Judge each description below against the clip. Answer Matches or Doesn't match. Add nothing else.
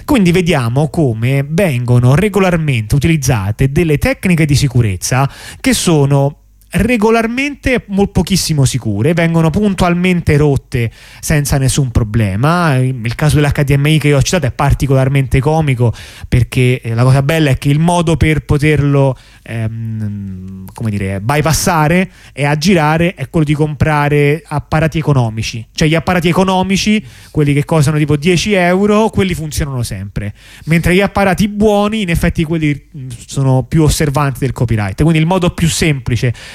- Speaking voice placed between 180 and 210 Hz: Doesn't match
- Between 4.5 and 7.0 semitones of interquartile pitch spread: Matches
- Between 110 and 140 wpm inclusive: Matches